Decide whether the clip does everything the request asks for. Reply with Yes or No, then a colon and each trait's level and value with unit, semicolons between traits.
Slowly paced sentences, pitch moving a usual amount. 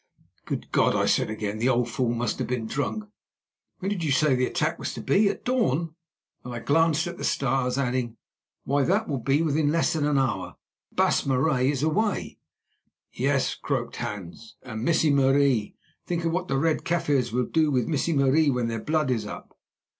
No: average, 195 wpm; average, 4.5 semitones